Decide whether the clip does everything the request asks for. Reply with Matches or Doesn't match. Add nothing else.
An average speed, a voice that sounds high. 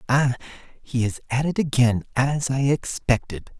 Doesn't match